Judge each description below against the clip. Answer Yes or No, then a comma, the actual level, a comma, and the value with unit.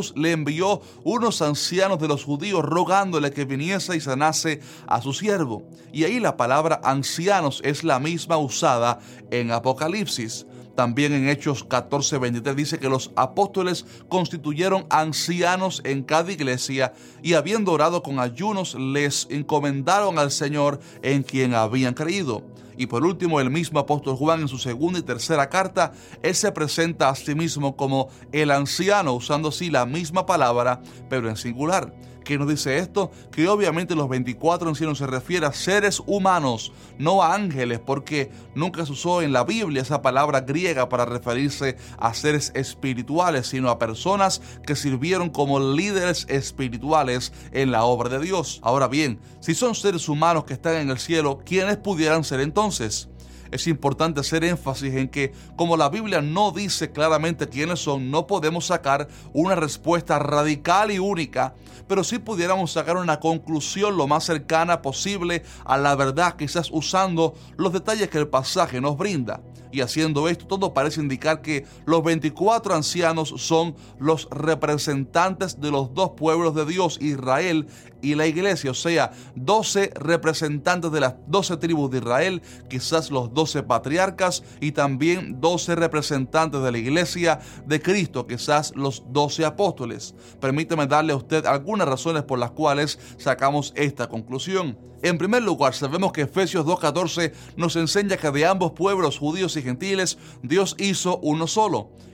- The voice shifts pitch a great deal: No, average, 4.3 semitones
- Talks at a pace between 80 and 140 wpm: No, average, 160 wpm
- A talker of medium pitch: Yes, medium, 150 Hz